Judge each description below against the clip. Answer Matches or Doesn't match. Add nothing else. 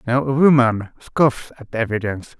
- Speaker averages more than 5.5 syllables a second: Doesn't match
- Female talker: Doesn't match